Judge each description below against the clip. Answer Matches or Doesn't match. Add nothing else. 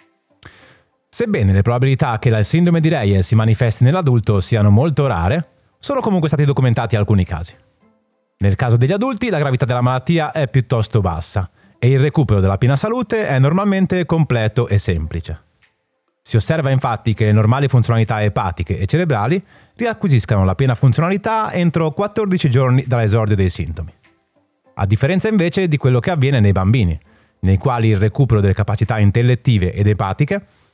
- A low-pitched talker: Matches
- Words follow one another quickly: Doesn't match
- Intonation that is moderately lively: Doesn't match